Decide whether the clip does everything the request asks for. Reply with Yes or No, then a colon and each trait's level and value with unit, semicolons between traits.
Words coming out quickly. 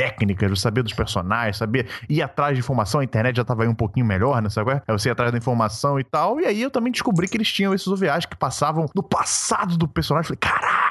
Yes: fast, 260 wpm